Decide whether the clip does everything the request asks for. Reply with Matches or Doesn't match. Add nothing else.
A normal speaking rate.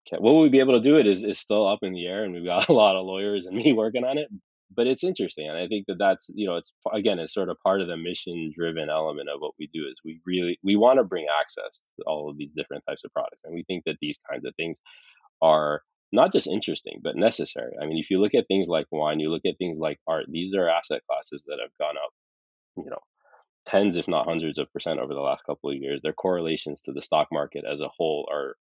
Doesn't match